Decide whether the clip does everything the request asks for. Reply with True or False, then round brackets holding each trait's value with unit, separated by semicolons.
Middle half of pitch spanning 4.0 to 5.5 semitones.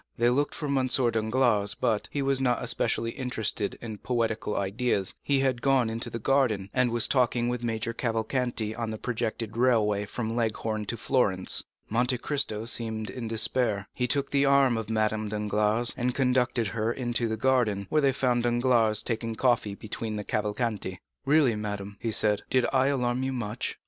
False (2.8 semitones)